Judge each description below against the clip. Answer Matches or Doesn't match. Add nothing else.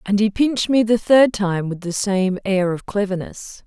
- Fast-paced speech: Matches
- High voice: Matches